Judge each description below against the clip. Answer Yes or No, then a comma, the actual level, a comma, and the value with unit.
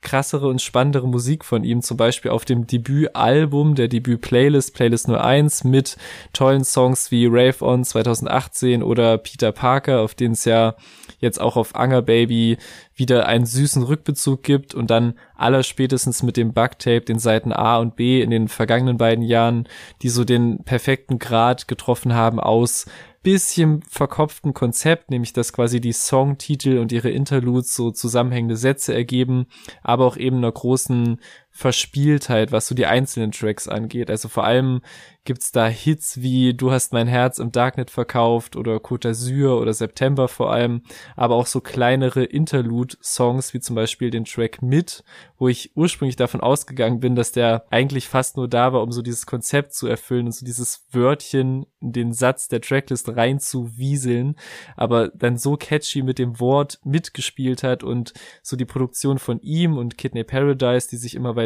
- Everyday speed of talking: Yes, average, 170 wpm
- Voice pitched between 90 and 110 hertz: No, low, 125 Hz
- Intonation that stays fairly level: Yes, narrow, 2.1 semitones